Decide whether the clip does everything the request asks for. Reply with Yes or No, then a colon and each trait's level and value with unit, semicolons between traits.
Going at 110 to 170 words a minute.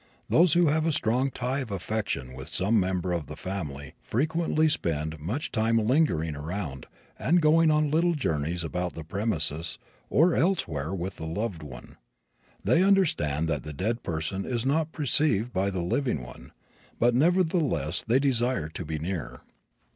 Yes: average, 160 wpm